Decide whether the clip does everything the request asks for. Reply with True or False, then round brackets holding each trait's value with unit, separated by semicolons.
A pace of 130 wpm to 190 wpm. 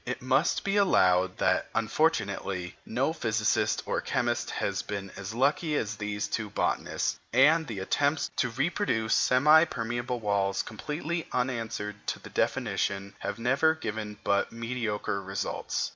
True (140 wpm)